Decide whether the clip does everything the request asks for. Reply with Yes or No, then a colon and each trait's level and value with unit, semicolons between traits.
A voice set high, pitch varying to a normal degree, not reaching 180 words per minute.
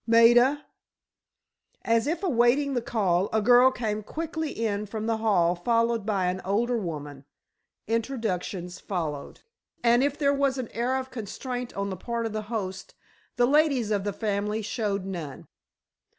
Yes: high, 225 Hz; average, 3.8 semitones; average, 155 wpm